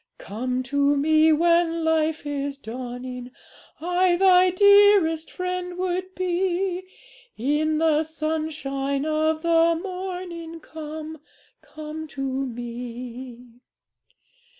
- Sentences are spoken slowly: Yes, slow, 95 wpm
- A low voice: No, very high, 315 Hz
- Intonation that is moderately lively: Yes, average, 4.2 semitones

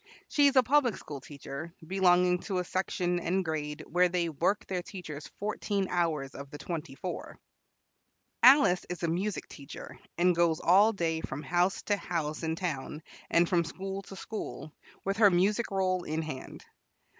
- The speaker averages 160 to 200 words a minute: Yes, average, 170 wpm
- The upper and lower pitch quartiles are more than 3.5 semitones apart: No, average, 3.2 semitones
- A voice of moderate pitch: Yes, medium, 175 Hz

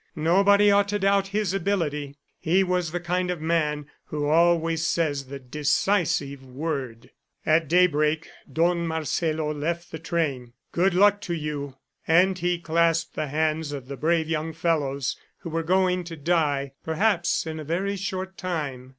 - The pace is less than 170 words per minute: Yes, average, 160 wpm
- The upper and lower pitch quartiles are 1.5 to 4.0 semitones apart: Yes, average, 3.1 semitones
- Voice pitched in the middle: Yes, medium, 165 Hz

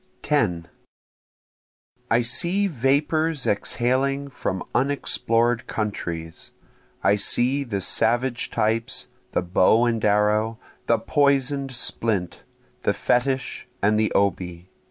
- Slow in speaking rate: Yes, slow, 100 wpm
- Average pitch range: Yes, average, 4.7 semitones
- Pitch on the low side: Yes, low, 115 Hz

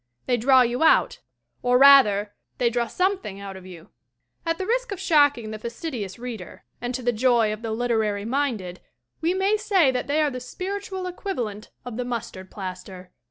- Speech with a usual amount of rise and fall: No, wide, 5.9 semitones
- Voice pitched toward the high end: Yes, high, 245 Hz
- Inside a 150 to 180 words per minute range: No, fast, 205 wpm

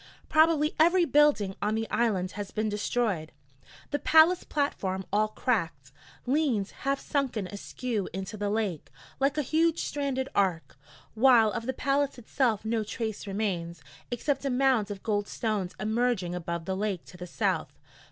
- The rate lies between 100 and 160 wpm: Yes, average, 155 wpm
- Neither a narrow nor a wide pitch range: No, wide, 5.7 semitones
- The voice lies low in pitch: No, high, 220 Hz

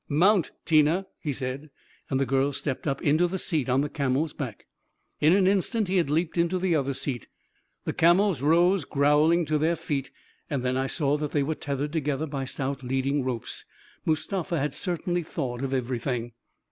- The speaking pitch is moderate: Yes, medium, 150 Hz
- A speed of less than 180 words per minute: No, average, 195 wpm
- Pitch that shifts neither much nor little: Yes, average, 3.9 semitones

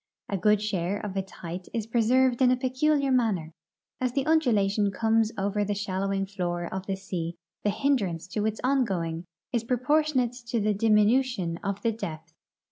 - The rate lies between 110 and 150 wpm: No, average, 175 wpm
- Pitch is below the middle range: No, high, 210 Hz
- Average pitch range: Yes, average, 4.6 semitones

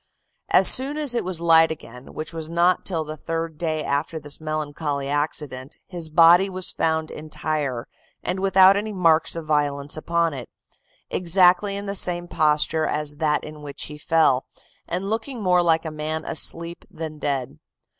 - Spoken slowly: No, average, 170 wpm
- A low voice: No, medium, 160 Hz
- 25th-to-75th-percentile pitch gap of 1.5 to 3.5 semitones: Yes, average, 2.9 semitones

